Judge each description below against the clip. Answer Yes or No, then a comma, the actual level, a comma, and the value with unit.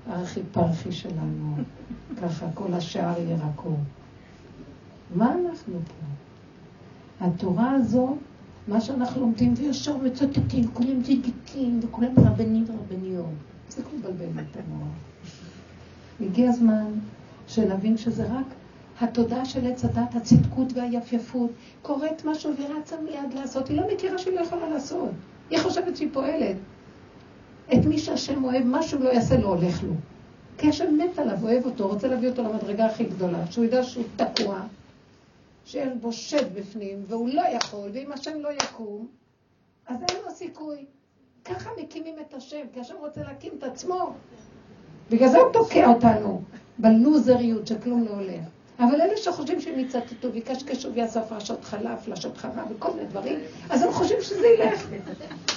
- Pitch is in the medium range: No, high, 240 Hz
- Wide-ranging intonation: Yes, wide, 5.7 semitones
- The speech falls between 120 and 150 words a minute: Yes, average, 145 wpm